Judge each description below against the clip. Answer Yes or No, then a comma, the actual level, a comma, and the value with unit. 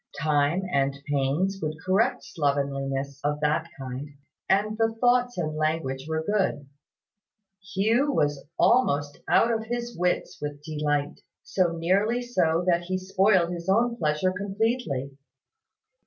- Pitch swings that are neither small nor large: No, wide, 5.9 semitones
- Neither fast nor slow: No, slow, 130 wpm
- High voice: No, medium, 170 Hz